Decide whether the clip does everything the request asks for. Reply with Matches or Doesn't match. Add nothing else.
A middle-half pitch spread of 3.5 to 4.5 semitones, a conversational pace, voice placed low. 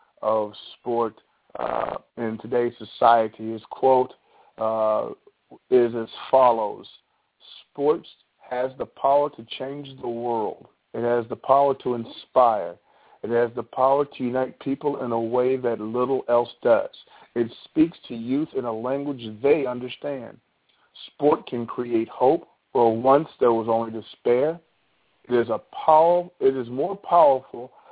Doesn't match